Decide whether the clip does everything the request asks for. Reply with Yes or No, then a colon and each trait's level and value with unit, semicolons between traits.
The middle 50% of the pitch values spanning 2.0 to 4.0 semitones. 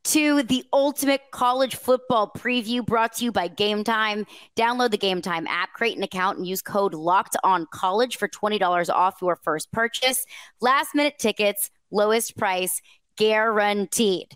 No: average, 4.5 semitones